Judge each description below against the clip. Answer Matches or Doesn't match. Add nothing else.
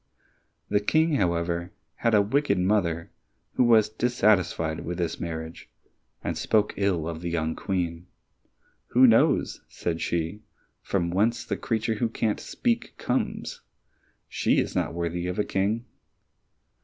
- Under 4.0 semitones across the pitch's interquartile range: Doesn't match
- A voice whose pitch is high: Doesn't match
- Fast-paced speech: Doesn't match